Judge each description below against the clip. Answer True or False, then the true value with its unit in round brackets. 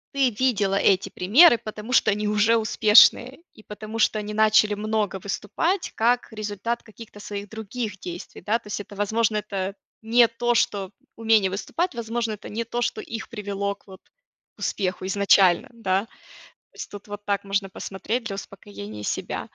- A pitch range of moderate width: False (2.3 semitones)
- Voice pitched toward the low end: False (210 Hz)